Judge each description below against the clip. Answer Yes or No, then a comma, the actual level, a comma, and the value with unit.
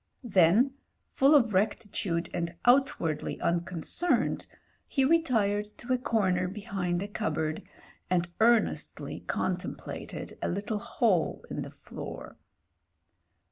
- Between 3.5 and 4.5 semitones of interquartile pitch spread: No, average, 5.1 semitones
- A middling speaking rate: No, slow, 105 wpm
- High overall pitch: Yes, high, 205 Hz